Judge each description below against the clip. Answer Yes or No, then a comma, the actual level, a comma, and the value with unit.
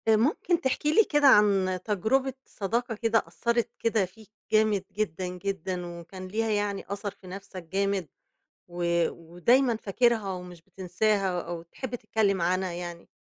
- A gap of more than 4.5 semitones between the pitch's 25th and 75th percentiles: No, average, 3.6 semitones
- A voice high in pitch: Yes, high, 200 Hz